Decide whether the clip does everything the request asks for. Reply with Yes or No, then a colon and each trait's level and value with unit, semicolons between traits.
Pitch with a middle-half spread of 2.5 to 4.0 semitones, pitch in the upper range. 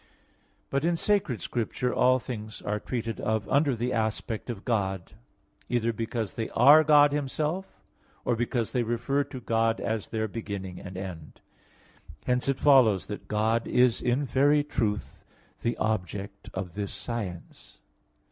No: average, 3.7 semitones; low, 115 Hz